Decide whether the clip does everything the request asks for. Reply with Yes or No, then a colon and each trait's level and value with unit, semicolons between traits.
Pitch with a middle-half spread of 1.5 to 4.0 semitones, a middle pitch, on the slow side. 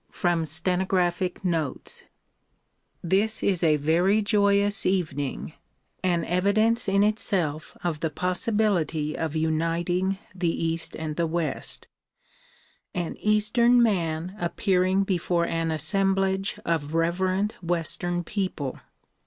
Yes: average, 3.1 semitones; medium, 175 Hz; slow, 105 wpm